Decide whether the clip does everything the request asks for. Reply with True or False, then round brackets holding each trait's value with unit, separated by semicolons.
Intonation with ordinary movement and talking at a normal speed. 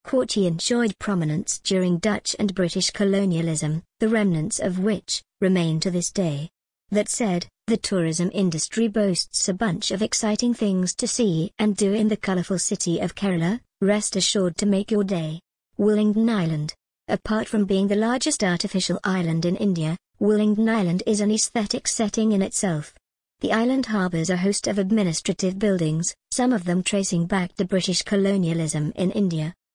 True (3.1 semitones; 160 wpm)